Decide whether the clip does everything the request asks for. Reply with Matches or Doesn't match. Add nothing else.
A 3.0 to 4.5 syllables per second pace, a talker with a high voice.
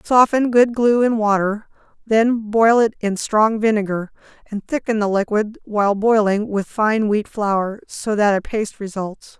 Matches